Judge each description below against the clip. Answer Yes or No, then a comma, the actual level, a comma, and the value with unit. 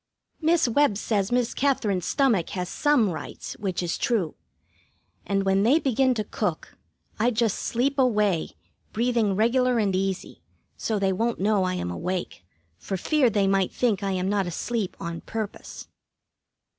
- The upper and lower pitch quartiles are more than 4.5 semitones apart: No, average, 4.2 semitones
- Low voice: No, high, 210 Hz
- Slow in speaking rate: No, average, 155 wpm